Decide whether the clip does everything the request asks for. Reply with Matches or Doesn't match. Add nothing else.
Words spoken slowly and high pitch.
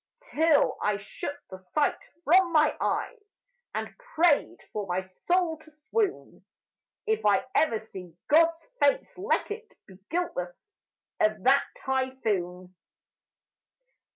Matches